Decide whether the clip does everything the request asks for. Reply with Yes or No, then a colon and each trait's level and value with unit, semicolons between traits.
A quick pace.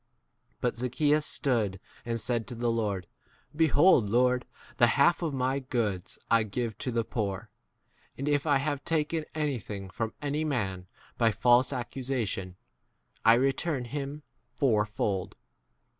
No: average, 145 wpm